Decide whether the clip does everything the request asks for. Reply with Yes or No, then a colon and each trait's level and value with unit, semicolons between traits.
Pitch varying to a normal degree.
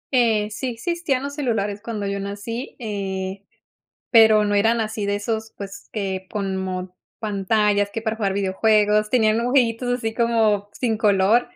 No: narrow, 2.3 semitones